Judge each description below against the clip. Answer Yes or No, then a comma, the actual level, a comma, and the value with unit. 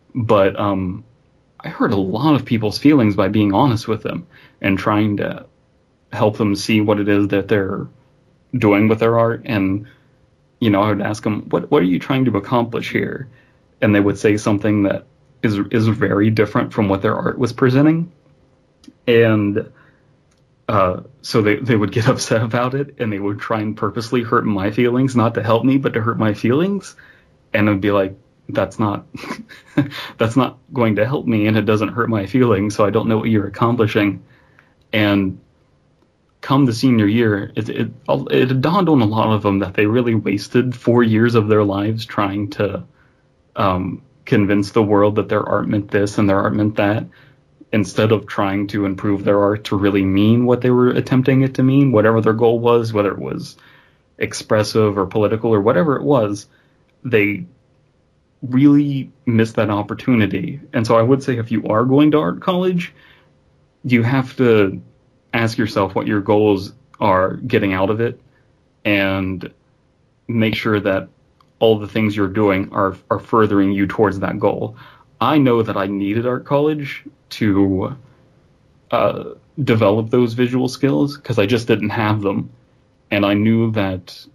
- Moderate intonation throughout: Yes, average, 3.5 semitones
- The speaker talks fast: No, average, 180 wpm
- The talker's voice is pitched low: Yes, low, 110 Hz